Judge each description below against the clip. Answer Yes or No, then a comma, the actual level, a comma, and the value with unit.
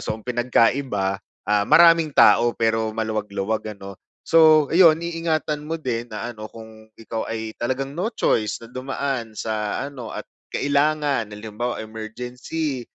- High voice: No, low, 120 Hz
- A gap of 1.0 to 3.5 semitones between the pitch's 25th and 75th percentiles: No, average, 4.7 semitones